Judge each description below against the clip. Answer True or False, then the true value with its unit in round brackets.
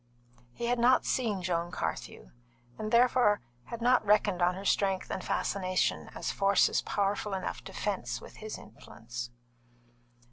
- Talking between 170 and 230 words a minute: False (145 wpm)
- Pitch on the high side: True (200 Hz)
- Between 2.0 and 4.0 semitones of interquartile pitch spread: True (3.1 semitones)